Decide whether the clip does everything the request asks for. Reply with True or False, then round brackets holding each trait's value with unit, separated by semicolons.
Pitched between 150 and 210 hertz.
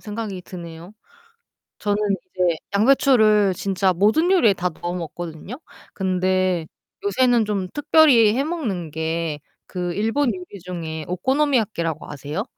True (190 Hz)